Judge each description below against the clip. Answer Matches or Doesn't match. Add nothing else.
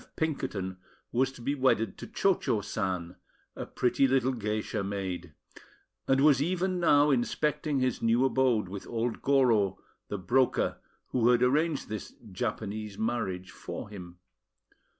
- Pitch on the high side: Doesn't match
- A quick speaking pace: Doesn't match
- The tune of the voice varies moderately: Matches